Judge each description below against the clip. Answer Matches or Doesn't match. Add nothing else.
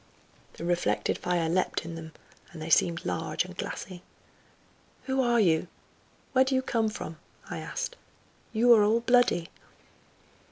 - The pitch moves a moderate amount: Doesn't match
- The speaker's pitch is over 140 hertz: Matches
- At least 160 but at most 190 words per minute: Doesn't match